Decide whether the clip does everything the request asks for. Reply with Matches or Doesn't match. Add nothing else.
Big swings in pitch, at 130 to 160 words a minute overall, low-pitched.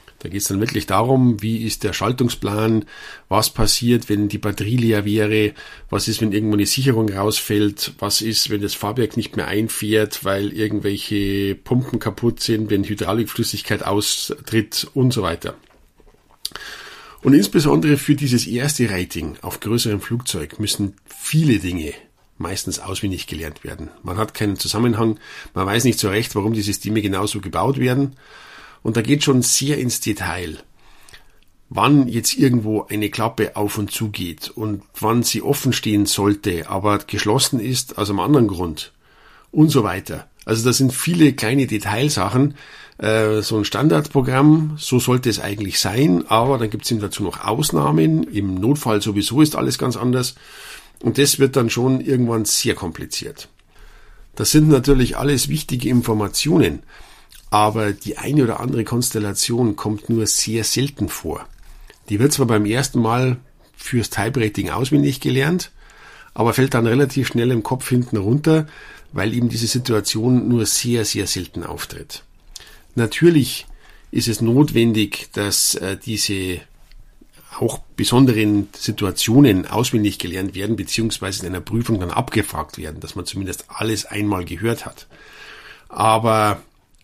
Doesn't match